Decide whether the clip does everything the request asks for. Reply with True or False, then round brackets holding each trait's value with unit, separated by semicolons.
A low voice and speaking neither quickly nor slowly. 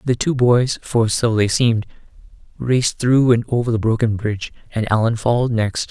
True (115 Hz; 165 wpm)